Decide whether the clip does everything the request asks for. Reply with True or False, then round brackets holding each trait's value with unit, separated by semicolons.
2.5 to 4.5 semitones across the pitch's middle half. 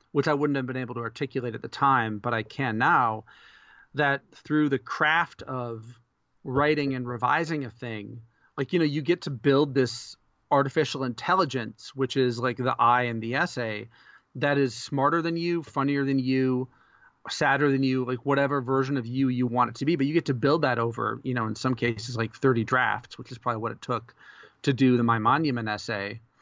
True (2.9 semitones)